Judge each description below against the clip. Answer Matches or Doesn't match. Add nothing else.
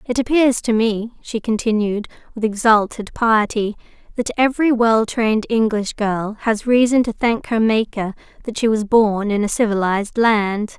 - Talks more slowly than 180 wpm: Matches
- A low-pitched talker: Doesn't match